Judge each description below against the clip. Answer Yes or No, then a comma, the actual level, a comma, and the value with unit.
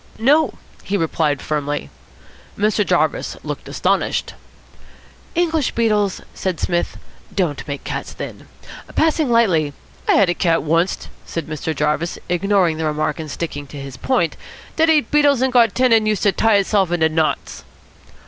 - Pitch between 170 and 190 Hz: Yes, medium, 185 Hz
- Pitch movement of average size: No, wide, 6.5 semitones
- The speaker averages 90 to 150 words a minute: No, average, 160 wpm